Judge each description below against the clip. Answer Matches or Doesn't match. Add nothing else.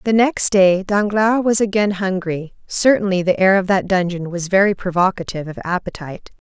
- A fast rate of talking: Doesn't match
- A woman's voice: Matches